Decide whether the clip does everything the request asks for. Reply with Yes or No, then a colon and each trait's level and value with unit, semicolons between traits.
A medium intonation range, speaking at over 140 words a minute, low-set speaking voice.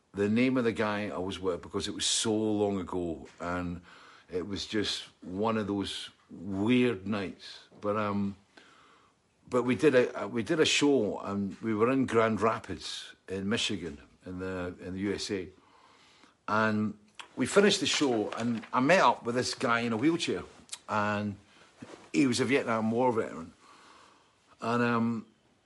Yes: average, 3.1 semitones; average, 165 wpm; low, 110 Hz